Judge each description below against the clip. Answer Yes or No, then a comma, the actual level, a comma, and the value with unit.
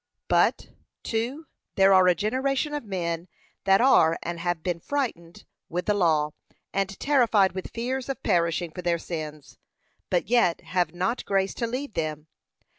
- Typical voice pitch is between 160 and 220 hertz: Yes, high, 190 Hz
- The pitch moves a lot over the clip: Yes, wide, 5.9 semitones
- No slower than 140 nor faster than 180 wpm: Yes, average, 160 wpm